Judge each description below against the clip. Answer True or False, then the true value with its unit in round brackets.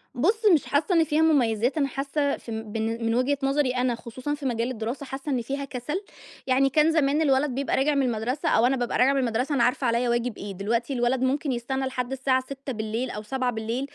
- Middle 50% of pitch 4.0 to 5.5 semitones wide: False (2.9 semitones)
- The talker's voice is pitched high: True (260 Hz)